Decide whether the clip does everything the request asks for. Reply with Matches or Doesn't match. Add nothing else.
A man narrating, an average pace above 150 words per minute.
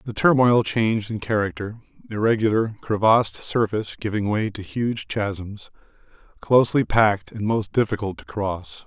Doesn't match